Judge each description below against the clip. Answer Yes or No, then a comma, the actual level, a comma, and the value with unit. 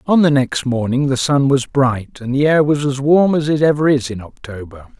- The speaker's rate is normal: No, fast, 240 wpm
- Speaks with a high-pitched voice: No, low, 135 Hz